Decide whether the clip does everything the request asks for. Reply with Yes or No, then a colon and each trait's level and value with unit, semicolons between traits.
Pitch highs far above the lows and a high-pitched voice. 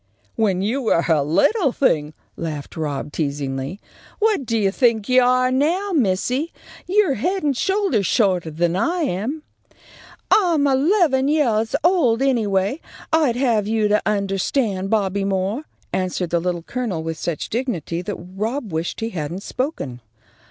Yes: wide, 7.3 semitones; high, 220 Hz